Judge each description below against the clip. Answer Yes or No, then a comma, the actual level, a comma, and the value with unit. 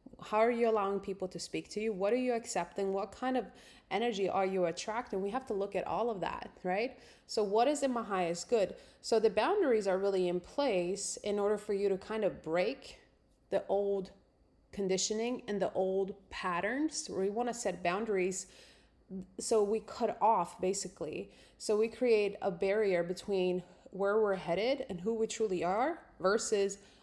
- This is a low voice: No, high, 200 Hz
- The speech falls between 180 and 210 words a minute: Yes, average, 185 wpm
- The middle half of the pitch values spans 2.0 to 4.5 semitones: Yes, average, 3.0 semitones